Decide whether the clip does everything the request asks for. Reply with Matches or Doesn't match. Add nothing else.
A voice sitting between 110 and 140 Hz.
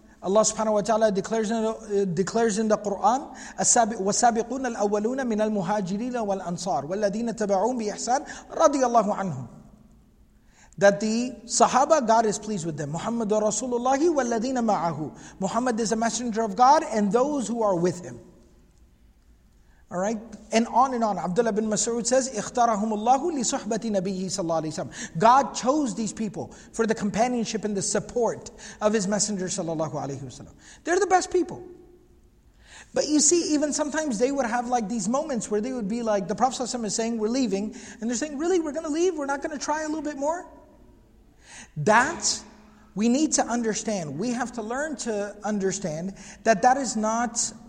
Doesn't match